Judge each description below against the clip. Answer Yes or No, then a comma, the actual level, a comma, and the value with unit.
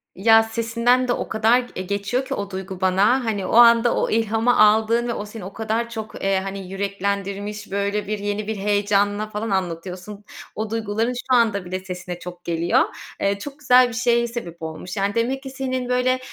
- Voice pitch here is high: Yes, high, 210 Hz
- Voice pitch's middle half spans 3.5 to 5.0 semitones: No, average, 3.1 semitones